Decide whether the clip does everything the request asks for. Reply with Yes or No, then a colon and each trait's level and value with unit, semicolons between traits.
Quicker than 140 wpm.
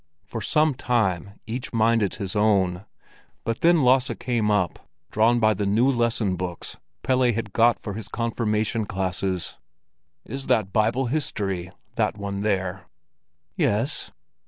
No: slow, 135 wpm